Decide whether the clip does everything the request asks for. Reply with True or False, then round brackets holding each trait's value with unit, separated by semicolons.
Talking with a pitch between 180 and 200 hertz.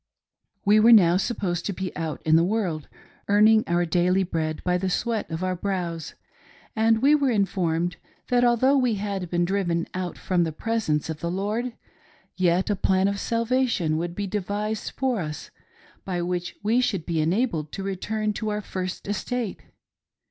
True (190 Hz)